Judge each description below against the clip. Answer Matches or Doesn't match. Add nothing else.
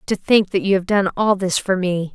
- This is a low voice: Doesn't match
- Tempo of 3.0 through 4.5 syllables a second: Doesn't match